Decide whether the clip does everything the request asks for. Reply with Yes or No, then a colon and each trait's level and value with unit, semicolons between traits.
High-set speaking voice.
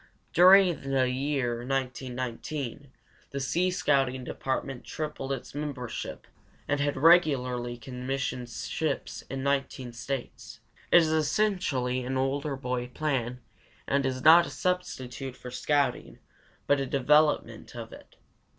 No: low, 135 Hz